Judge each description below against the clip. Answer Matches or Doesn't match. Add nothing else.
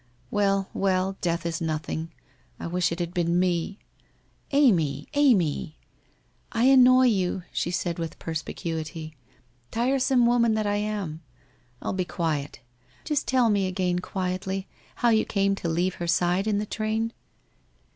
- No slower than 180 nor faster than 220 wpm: Doesn't match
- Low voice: Doesn't match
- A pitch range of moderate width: Matches